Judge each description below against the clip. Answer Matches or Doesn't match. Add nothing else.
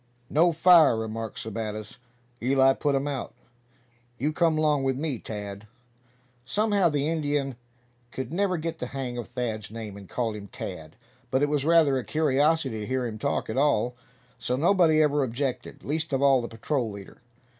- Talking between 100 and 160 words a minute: Doesn't match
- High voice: Doesn't match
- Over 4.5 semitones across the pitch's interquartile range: Matches